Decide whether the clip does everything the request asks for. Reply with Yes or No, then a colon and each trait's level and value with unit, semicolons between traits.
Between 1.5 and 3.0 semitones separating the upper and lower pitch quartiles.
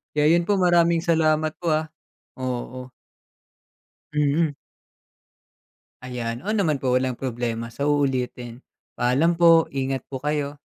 No: average, 4.3 semitones